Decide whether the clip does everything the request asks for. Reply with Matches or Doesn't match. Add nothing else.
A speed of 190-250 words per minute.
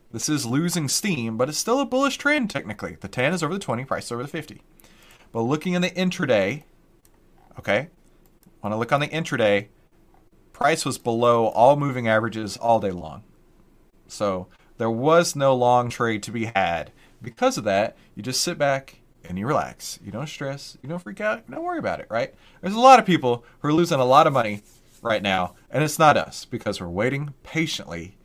Matches